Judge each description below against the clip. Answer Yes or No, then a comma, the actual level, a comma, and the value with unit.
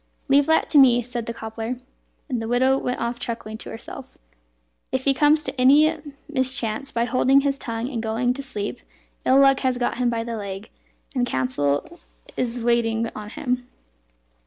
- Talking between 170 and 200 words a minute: Yes, average, 180 wpm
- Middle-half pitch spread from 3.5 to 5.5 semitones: No, average, 2.8 semitones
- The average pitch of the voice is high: Yes, high, 245 Hz